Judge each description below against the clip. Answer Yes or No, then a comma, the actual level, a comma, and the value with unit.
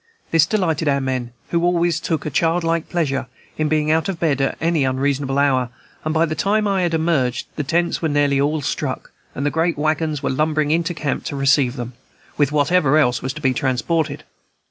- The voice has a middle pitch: Yes, medium, 155 Hz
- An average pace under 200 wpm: No, fast, 205 wpm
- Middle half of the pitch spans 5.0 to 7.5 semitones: No, average, 3.1 semitones